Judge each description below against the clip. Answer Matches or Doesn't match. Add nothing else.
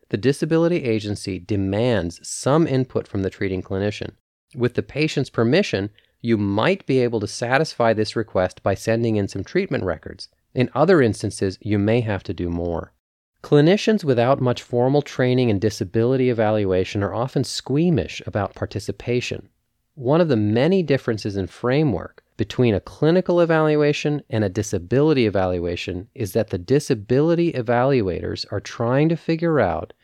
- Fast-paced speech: Doesn't match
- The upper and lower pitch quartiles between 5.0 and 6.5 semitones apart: Matches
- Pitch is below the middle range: Matches